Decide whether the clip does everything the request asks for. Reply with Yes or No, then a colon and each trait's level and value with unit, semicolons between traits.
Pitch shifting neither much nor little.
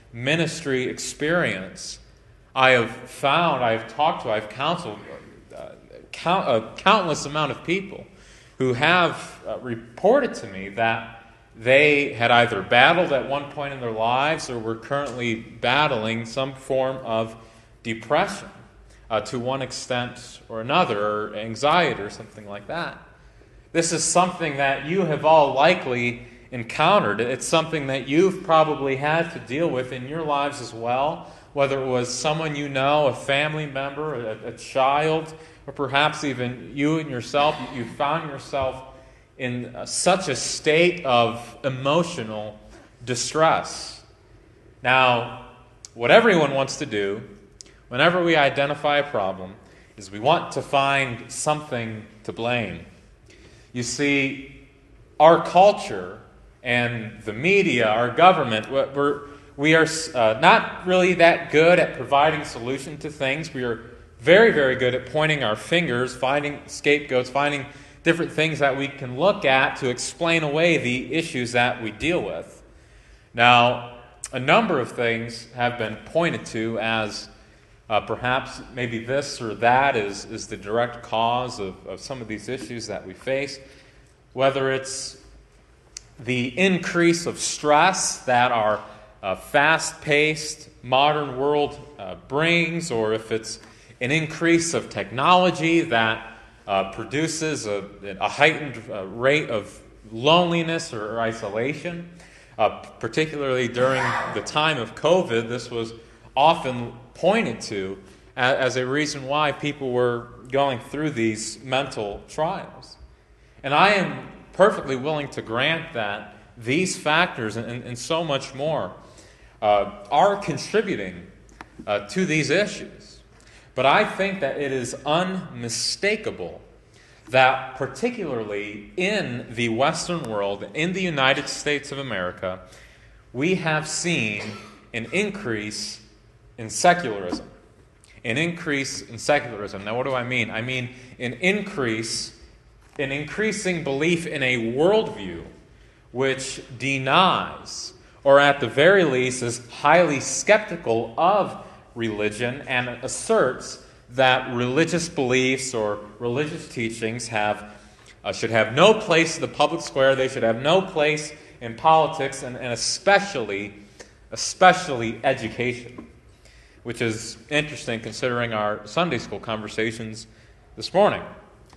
Yes: average, 4.9 semitones